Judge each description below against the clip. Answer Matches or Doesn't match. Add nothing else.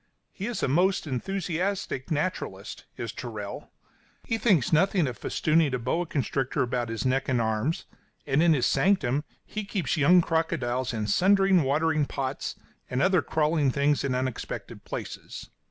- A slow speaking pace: Doesn't match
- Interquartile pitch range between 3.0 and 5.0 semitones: Doesn't match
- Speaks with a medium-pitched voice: Matches